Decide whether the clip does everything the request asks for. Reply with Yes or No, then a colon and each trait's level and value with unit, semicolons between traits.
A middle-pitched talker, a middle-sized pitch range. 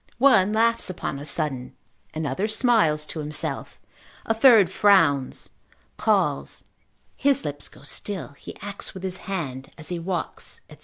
No: medium, 180 Hz; wide, 5.9 semitones